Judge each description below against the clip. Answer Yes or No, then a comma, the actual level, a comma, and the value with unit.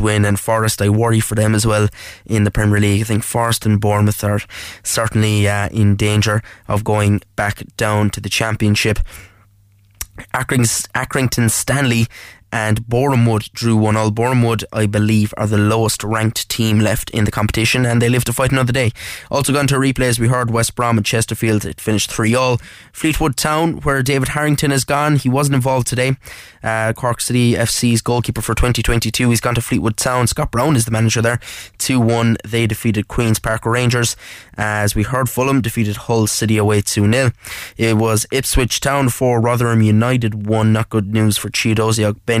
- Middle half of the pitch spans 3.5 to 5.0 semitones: No, average, 2.7 semitones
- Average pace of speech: Yes, average, 185 wpm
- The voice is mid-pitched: No, low, 115 Hz